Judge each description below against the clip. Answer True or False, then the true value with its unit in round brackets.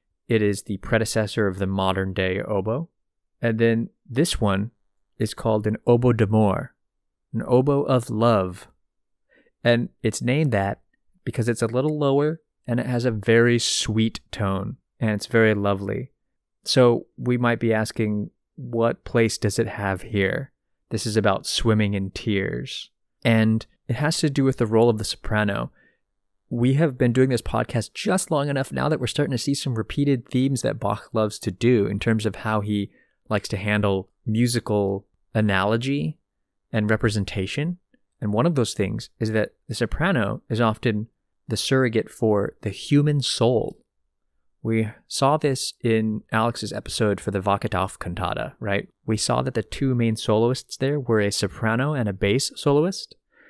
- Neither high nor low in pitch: False (110 Hz)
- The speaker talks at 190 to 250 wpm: False (165 wpm)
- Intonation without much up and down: False (3.4 semitones)